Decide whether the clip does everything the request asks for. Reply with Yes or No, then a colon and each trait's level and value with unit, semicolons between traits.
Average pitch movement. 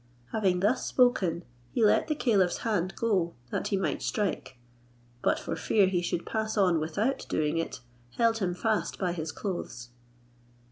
Yes: average, 4.3 semitones